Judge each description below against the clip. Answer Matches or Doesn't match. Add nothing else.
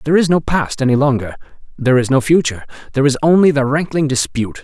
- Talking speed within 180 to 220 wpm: Matches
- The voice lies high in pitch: Doesn't match